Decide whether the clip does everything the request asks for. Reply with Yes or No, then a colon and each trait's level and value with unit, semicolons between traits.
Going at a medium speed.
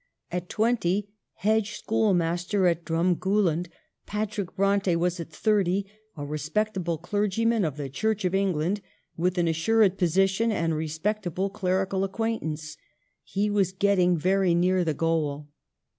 No: slow, 130 wpm